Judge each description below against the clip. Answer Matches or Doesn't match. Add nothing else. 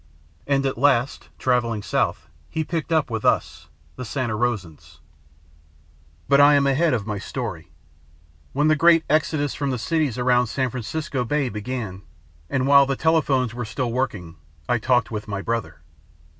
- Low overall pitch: Matches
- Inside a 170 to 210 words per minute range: Doesn't match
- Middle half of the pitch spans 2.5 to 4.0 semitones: Doesn't match